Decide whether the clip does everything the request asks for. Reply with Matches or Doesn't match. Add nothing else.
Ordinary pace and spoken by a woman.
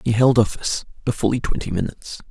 Doesn't match